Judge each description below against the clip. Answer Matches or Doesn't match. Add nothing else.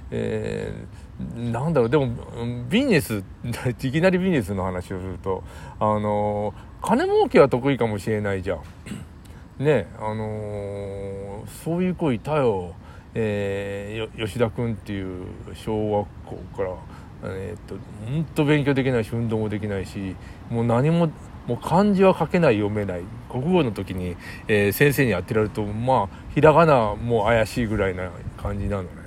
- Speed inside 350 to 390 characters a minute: Doesn't match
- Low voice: Matches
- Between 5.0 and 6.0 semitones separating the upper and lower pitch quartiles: Doesn't match